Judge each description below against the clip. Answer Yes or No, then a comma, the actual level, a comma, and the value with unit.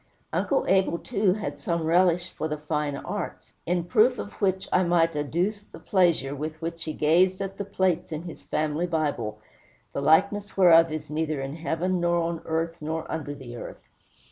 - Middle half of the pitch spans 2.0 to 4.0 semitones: Yes, average, 3.1 semitones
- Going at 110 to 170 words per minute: No, average, 185 wpm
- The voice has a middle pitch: Yes, medium, 165 Hz